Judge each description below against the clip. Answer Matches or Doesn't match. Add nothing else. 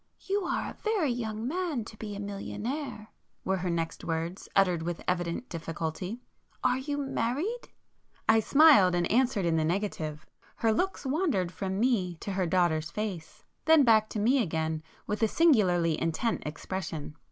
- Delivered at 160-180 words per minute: Doesn't match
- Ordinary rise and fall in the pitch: Doesn't match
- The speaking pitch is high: Matches